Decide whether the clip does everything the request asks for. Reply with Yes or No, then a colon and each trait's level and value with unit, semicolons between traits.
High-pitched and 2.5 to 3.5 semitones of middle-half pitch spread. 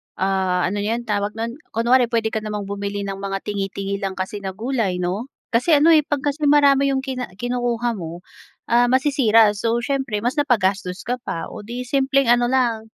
No: high, 230 Hz; average, 4.4 semitones